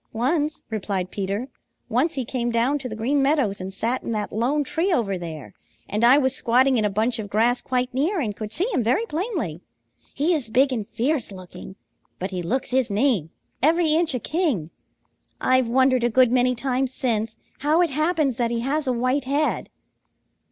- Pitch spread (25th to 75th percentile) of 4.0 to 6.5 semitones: Yes, average, 4.6 semitones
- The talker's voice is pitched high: Yes, very high, 250 Hz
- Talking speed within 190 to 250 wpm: Yes, average, 195 wpm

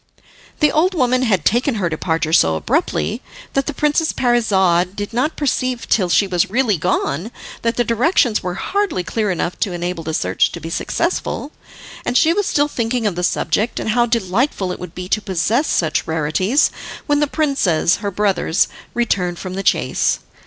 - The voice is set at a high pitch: Yes, high, 210 Hz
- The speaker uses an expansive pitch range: Yes, wide, 6.2 semitones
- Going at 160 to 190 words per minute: Yes, average, 180 wpm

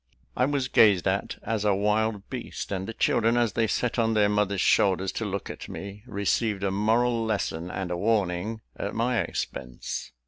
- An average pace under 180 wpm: No, average, 185 wpm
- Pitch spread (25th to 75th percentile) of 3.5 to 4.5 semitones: No, narrow, 2.6 semitones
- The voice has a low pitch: Yes, low, 105 Hz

